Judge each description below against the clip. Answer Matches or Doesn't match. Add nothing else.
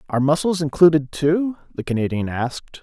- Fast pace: Doesn't match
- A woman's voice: Doesn't match